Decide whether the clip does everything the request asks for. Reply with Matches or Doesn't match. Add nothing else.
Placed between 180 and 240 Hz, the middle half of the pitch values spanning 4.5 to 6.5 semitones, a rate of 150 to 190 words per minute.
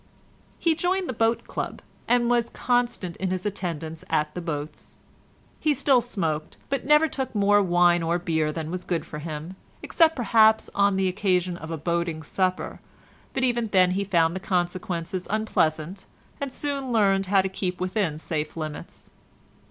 Matches